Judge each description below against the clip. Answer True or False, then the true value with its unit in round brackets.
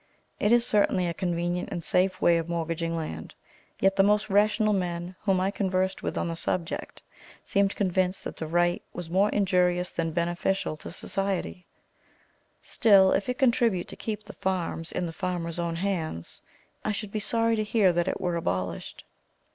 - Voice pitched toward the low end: False (185 Hz)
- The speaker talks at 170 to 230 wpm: True (180 wpm)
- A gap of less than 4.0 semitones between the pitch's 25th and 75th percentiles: True (2.8 semitones)